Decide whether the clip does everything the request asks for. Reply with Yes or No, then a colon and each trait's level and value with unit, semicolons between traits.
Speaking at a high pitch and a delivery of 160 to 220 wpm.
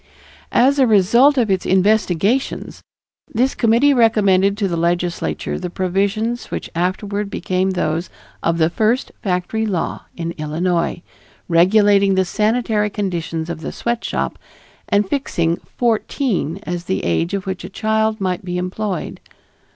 No: high, 195 Hz; slow, 135 wpm